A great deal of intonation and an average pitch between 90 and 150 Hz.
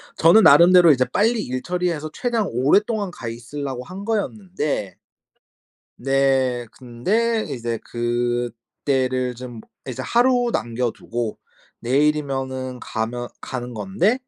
Yes: wide, 7.2 semitones; low, 135 Hz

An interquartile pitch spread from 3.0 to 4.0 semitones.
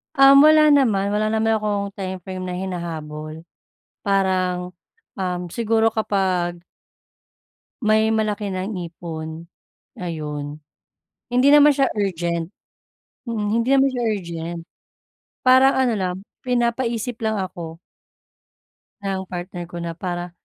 No: average, 4.4 semitones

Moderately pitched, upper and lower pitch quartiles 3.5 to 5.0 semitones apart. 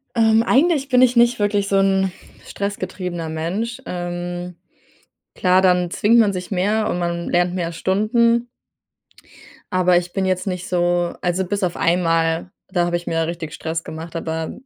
No: medium, 180 Hz; average, 3.0 semitones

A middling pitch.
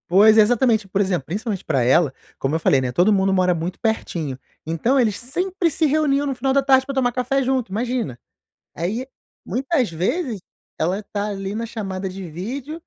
No: high, 215 Hz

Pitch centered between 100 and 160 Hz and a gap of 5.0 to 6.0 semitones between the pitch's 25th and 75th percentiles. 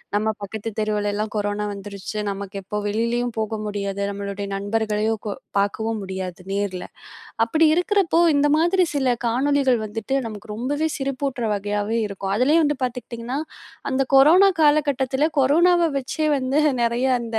No: high, 225 Hz; average, 5.3 semitones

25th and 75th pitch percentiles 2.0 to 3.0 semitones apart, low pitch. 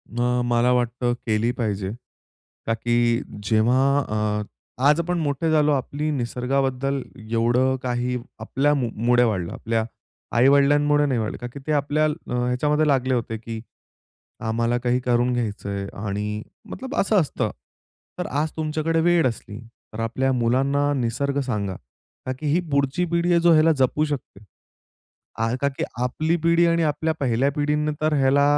No: average, 4.0 semitones; low, 130 Hz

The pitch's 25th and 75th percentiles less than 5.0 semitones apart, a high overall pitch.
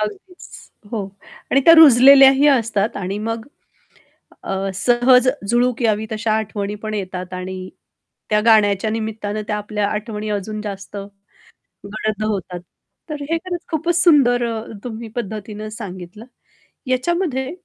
Yes: average, 3.6 semitones; high, 220 Hz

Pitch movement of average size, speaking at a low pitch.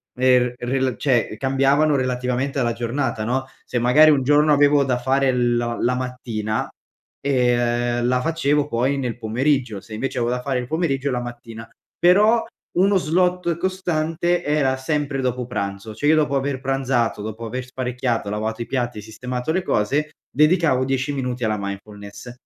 Yes: average, 3.2 semitones; low, 130 Hz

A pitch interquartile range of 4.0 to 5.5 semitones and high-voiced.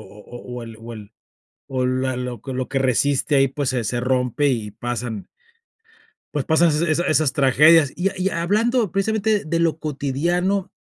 No: average, 5.1 semitones; medium, 140 Hz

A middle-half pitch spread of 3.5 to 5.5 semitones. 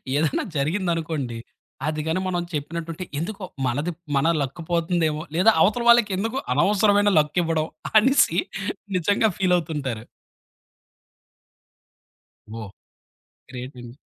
Yes: average, 4.4 semitones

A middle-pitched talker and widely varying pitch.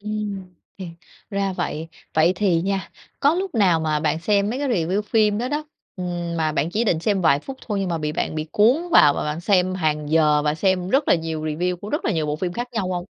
No: medium, 180 Hz; average, 4.8 semitones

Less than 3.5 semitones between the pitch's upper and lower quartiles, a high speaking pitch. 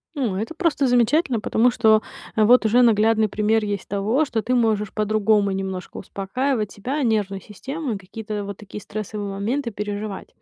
Yes: average, 3.0 semitones; high, 215 Hz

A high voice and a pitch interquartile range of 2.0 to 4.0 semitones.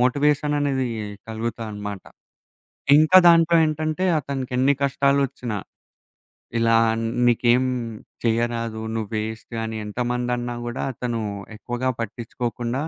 No: low, 120 Hz; average, 3.3 semitones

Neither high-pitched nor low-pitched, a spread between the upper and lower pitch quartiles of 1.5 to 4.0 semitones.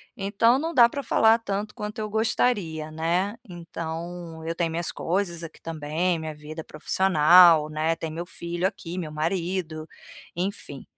Yes: medium, 170 Hz; average, 3.6 semitones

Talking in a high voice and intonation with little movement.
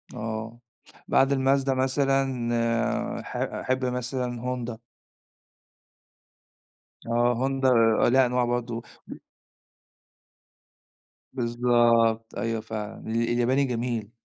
No: low, 120 Hz; narrow, 2.1 semitones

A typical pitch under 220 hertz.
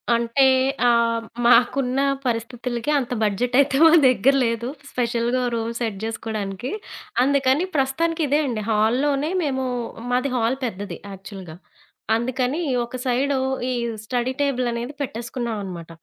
No: high, 245 Hz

